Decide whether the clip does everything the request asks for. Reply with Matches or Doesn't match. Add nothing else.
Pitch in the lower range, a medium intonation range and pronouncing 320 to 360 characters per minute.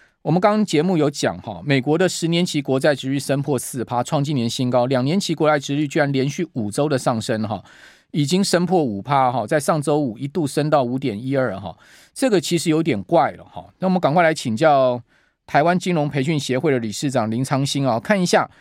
Doesn't match